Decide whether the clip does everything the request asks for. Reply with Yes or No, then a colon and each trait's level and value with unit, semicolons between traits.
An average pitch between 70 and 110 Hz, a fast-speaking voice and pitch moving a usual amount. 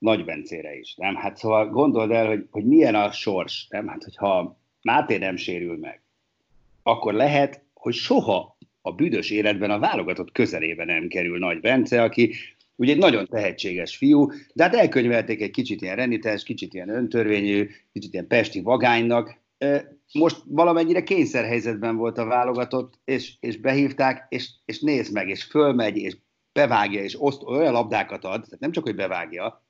No: low, 120 Hz; fast, 165 wpm; average, 4.6 semitones